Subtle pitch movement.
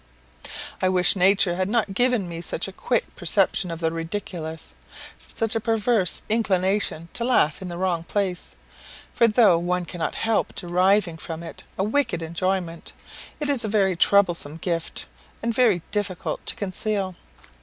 No: average, 3.6 semitones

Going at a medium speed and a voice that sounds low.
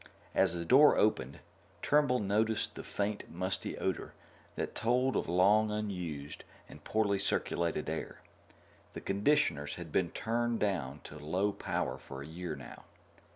Yes: average, 145 wpm; very low, 95 Hz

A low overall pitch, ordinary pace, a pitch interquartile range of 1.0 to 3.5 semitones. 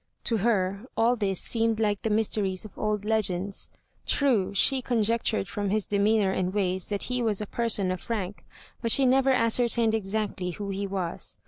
No: high, 210 Hz; average, 180 wpm; average, 2.8 semitones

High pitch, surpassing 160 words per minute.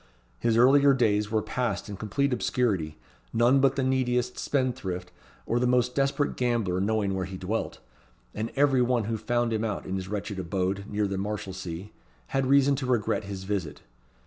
No: low, 110 Hz; average, 175 wpm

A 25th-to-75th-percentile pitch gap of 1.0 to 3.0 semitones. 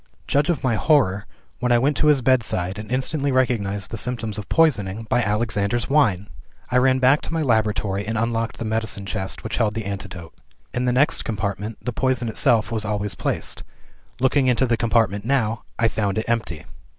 No: average, 3.7 semitones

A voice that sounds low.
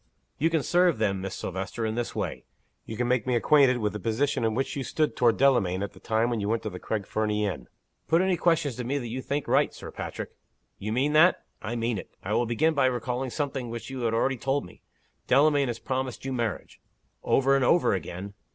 Yes: low, 120 Hz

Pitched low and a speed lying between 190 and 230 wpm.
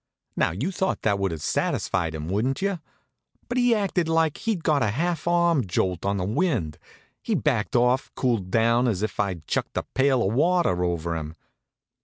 Yes: low, 120 Hz; average, 195 wpm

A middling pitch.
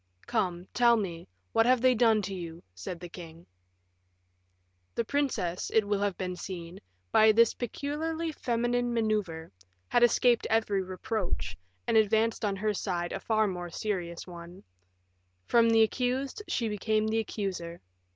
No: high, 215 Hz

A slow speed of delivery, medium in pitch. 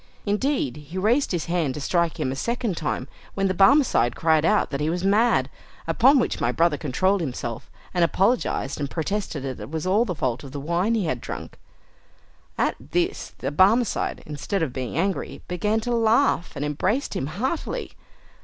No: average, 185 wpm; medium, 175 Hz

